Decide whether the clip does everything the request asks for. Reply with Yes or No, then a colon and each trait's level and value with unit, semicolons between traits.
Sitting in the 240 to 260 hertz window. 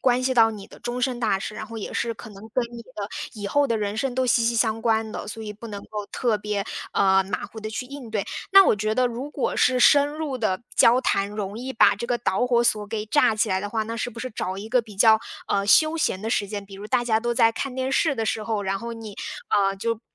No: high, 225 Hz